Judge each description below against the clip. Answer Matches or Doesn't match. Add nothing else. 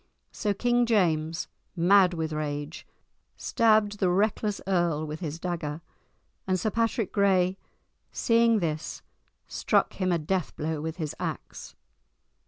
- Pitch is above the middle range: Doesn't match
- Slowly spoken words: Matches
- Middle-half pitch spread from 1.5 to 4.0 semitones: Doesn't match